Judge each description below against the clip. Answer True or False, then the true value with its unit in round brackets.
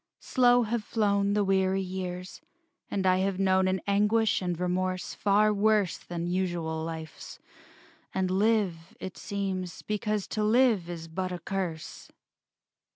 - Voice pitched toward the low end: False (190 Hz)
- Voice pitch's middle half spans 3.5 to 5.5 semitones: False (2.5 semitones)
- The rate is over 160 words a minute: False (140 wpm)